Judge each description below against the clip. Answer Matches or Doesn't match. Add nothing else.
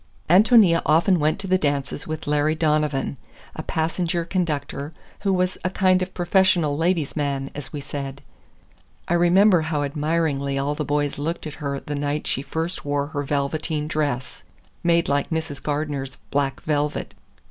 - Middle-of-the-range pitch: Matches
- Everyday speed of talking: Matches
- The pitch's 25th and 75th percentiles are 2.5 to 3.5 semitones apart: Matches